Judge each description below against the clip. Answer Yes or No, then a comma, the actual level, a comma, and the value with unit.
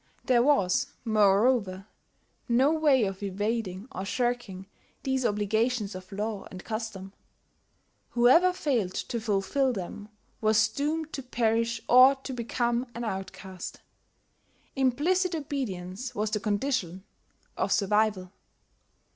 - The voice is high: Yes, high, 225 Hz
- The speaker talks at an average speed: No, slow, 115 wpm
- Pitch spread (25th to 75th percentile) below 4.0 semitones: No, average, 4.6 semitones